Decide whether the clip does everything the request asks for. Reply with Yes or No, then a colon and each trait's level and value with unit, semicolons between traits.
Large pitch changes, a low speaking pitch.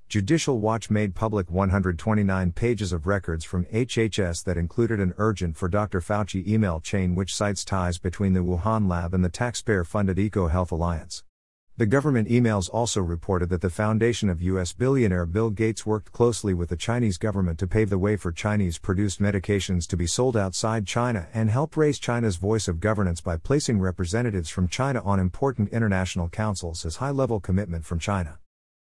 No: average, 3.6 semitones; low, 100 Hz